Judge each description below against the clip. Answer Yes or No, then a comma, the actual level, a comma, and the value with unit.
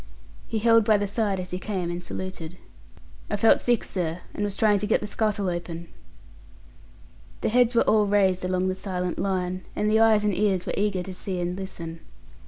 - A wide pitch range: No, narrow, 2.6 semitones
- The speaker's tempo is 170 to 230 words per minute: Yes, average, 195 wpm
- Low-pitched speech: No, high, 195 Hz